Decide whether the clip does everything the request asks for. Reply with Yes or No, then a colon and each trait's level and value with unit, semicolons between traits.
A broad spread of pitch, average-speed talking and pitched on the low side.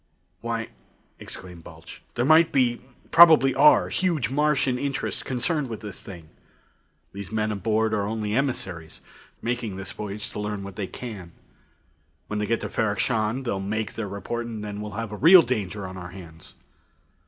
No: average, 4.0 semitones; average, 170 wpm; low, 110 Hz